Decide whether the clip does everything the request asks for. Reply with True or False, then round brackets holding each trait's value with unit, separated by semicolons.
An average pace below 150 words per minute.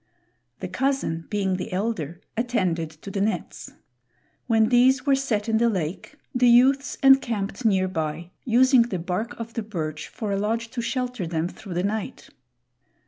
False (165 wpm)